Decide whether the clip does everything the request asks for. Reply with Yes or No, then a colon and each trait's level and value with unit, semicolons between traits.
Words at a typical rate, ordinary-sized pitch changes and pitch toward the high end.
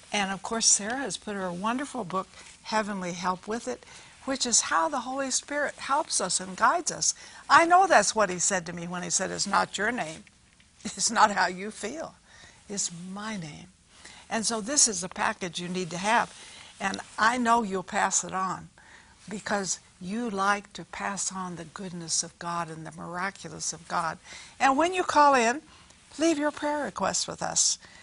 Yes: average, 195 wpm; average, 4.8 semitones; high, 205 Hz